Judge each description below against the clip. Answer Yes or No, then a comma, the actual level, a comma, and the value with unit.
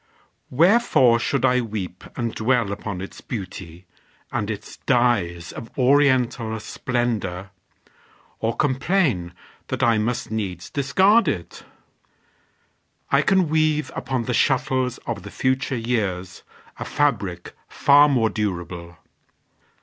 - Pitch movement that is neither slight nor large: Yes, average, 5.0 semitones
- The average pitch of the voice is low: Yes, low, 120 Hz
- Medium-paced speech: No, slow, 115 wpm